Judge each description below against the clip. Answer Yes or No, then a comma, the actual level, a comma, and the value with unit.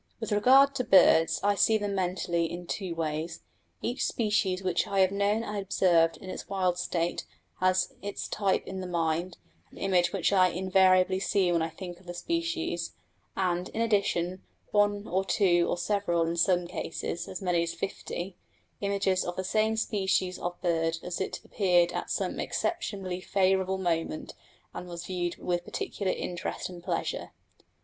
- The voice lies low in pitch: No, medium, 185 Hz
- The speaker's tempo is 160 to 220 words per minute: Yes, average, 170 wpm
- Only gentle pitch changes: Yes, narrow, 2.3 semitones